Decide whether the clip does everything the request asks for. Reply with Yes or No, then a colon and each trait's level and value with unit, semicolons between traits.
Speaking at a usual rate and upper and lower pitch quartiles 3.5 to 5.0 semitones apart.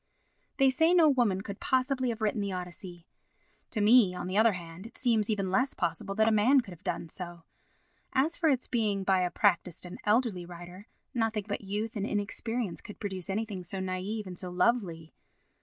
Yes: average, 195 wpm; average, 4.0 semitones